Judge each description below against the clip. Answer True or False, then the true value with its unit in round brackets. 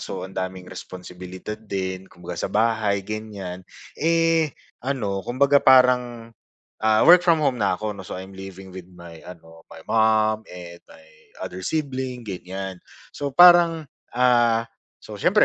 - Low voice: True (110 Hz)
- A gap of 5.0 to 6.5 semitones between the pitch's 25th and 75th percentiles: True (5.6 semitones)